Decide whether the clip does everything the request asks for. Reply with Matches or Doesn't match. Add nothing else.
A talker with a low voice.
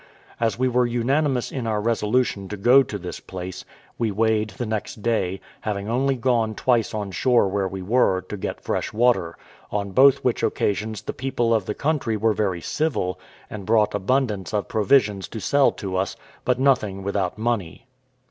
Matches